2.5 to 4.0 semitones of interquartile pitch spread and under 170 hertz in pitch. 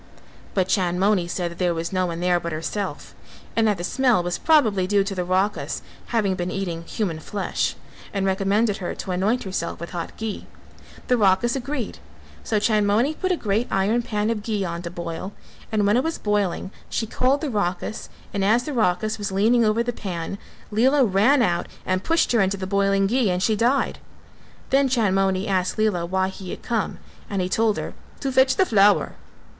No: average, 3.6 semitones; high, 200 Hz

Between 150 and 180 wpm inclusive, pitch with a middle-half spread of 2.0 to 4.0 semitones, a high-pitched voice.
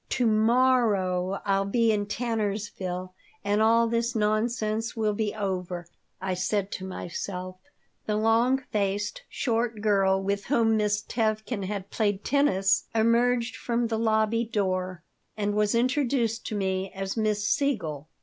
No: average, 140 wpm; average, 2.9 semitones; high, 210 Hz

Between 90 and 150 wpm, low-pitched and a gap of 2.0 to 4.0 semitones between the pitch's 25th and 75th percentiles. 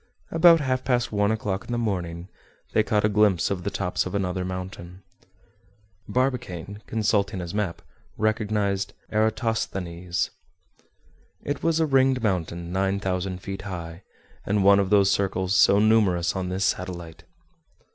Yes: average, 145 wpm; low, 100 Hz; average, 2.9 semitones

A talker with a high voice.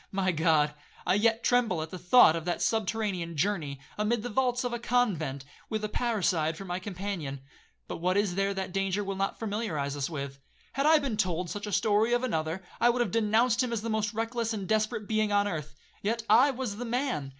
Yes: high, 205 Hz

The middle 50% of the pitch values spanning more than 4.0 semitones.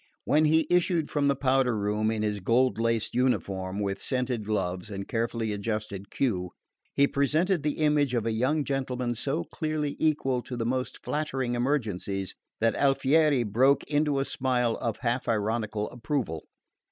Yes: average, 4.6 semitones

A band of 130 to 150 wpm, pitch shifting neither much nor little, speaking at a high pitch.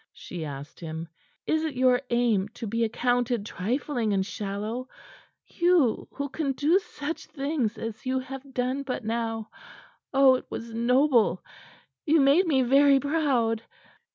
Yes: average, 145 wpm; average, 3.9 semitones; very high, 250 Hz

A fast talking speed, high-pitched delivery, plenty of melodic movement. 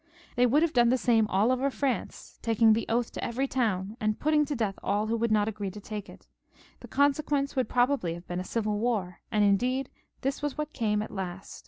No: fast, 230 wpm; high, 230 Hz; average, 4.1 semitones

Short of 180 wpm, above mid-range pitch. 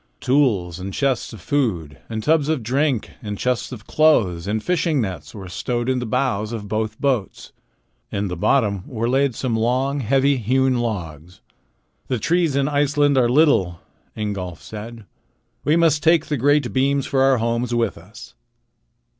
No: average, 165 wpm; low, 120 Hz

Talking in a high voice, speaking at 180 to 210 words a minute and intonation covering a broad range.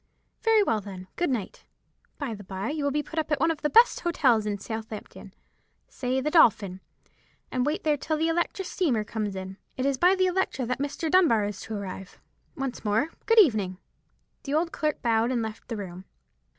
Yes: very high, 255 Hz; average, 190 wpm; wide, 7.1 semitones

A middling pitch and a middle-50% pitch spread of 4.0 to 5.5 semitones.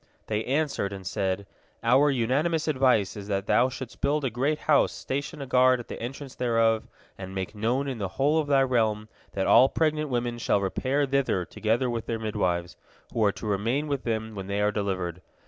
No: low, 120 Hz; average, 4.8 semitones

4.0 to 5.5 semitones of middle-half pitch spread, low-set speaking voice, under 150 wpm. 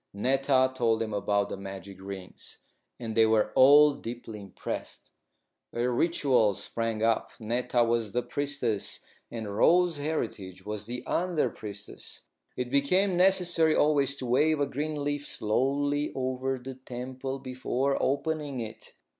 Yes: average, 4.4 semitones; low, 130 Hz; average, 140 wpm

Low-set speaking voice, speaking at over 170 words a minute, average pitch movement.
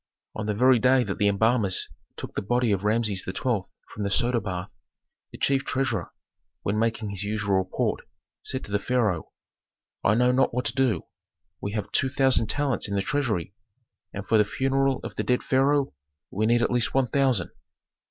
Yes: low, 115 Hz; average, 190 wpm; average, 4.2 semitones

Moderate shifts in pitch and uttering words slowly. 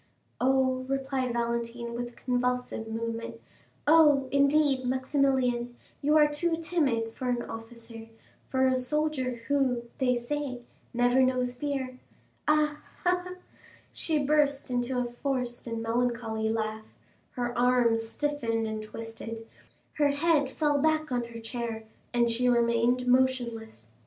Yes: average, 3.0 semitones; slow, 130 wpm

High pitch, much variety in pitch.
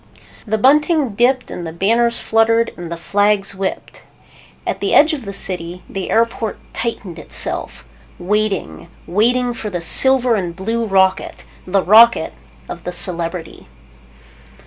No: high, 210 Hz; average, 4.2 semitones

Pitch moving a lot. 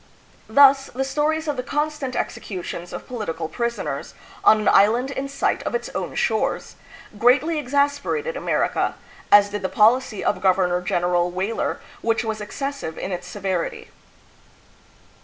Yes: wide, 6.6 semitones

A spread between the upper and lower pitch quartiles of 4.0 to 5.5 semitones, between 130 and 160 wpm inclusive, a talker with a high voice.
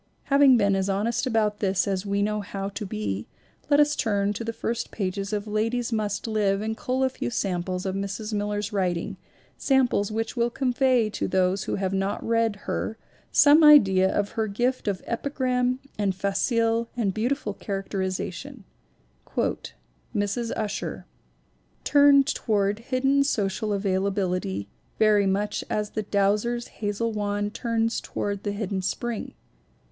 No: average, 3.0 semitones; average, 150 wpm; high, 210 Hz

